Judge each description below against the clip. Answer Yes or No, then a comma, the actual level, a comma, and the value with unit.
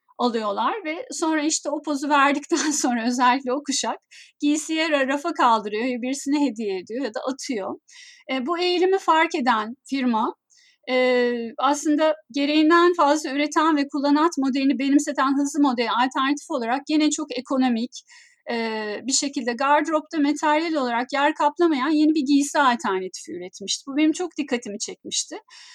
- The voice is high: Yes, very high, 285 Hz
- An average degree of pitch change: Yes, average, 3.7 semitones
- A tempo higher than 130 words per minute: Yes, fast, 140 wpm